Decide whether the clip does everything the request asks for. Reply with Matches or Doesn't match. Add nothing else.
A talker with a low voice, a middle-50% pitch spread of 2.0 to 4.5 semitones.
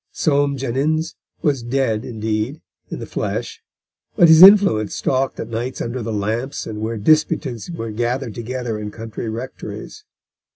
Matches